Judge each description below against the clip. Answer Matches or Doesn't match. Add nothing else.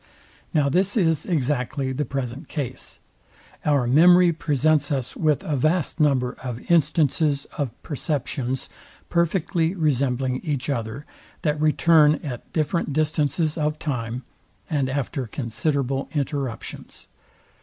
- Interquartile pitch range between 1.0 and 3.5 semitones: Matches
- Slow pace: Matches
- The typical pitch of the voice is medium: Matches